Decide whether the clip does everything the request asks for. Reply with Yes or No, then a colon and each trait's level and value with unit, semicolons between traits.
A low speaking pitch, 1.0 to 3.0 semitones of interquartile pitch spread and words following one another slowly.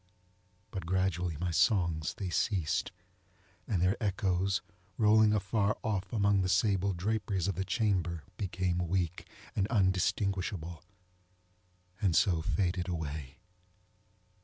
Yes: very low, 95 Hz; narrow, 2.5 semitones; slow, 110 wpm